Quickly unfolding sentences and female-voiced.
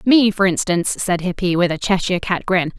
Yes: fast, 215 wpm; female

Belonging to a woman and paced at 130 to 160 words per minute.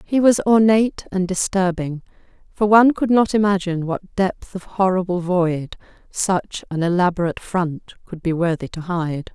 Yes: female; average, 155 wpm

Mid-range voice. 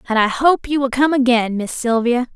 No: very high, 250 Hz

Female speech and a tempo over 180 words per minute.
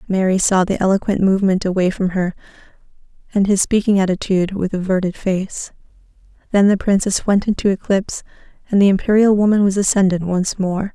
No: female; average, 160 wpm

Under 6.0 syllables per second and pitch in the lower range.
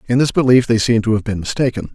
No: 6.9 syllables/s; low, 115 Hz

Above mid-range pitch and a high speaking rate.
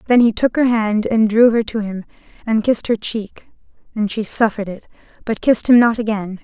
Yes: high, 220 Hz; fast, 215 wpm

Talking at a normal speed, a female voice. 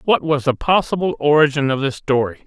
No: average, 195 wpm; male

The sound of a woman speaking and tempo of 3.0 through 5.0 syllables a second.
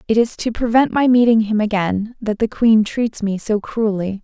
Yes: female; 4.7 syllables/s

